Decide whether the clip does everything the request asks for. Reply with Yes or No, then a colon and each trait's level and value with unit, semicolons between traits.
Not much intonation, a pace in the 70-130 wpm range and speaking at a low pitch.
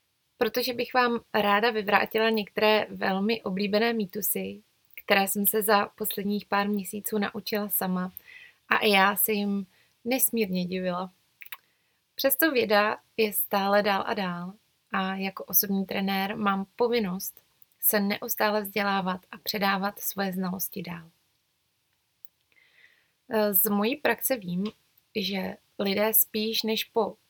No: narrow, 2.2 semitones; average, 120 wpm; high, 205 Hz